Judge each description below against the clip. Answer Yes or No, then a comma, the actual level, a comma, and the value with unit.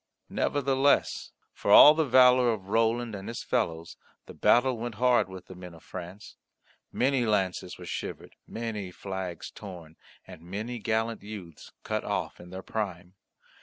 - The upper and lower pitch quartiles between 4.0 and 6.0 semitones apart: Yes, average, 4.7 semitones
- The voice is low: Yes, low, 105 Hz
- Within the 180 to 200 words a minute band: No, average, 155 wpm